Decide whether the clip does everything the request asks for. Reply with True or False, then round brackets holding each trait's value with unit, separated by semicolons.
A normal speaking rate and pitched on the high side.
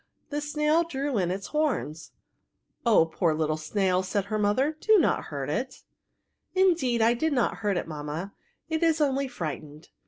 True (180 wpm; 225 Hz)